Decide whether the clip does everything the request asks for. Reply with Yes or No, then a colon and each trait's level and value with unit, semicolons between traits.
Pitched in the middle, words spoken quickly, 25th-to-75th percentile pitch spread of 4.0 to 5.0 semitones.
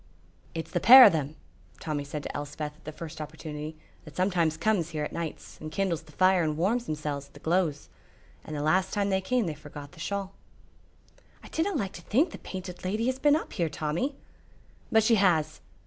Yes: medium, 170 Hz; fast, 210 wpm; average, 4.5 semitones